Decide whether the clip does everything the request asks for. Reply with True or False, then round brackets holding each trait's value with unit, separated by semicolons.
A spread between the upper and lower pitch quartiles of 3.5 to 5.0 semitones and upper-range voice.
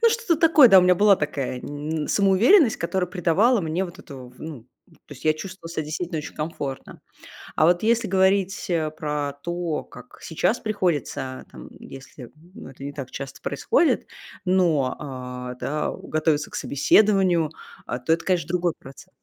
False (4.7 semitones; 165 Hz)